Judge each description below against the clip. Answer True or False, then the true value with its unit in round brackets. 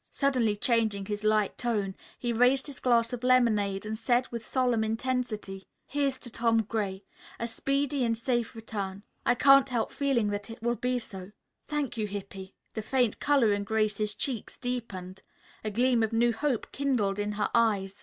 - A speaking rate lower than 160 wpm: False (175 wpm)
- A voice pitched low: False (230 Hz)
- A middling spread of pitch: True (3.3 semitones)